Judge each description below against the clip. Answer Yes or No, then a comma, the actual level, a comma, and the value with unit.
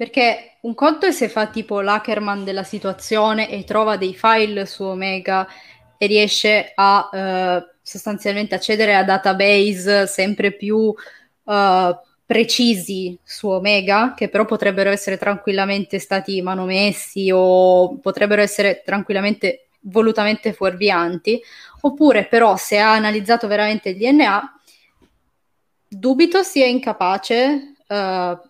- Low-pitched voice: No, high, 205 Hz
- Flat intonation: Yes, narrow, 2.3 semitones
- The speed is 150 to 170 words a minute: No, slow, 115 wpm